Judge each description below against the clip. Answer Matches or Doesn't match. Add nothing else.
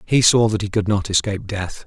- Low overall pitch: Matches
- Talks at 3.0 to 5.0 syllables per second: Doesn't match